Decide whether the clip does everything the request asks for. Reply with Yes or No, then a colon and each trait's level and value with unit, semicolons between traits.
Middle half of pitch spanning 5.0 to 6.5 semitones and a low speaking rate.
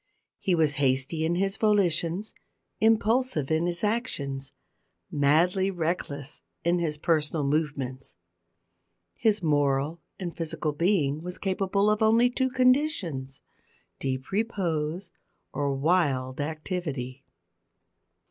Yes: wide, 5.5 semitones; slow, 105 wpm